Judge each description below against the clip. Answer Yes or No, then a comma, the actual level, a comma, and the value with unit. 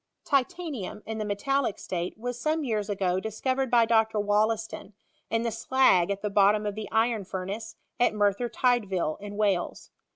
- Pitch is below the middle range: No, high, 215 Hz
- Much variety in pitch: No, average, 3.0 semitones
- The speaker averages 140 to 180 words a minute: Yes, average, 165 wpm